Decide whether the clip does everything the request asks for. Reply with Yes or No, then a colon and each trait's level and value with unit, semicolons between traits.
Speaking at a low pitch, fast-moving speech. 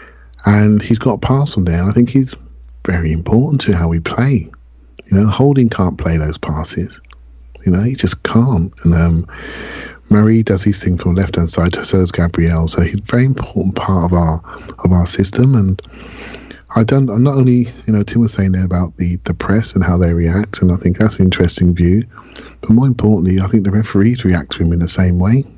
Yes: very low, 95 Hz; fast, 225 wpm